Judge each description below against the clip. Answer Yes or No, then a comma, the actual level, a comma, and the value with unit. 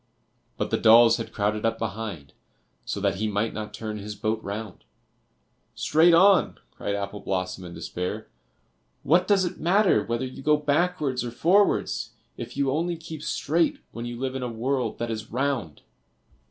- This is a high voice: No, low, 120 Hz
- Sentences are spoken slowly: No, average, 170 wpm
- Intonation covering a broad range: Yes, wide, 6.1 semitones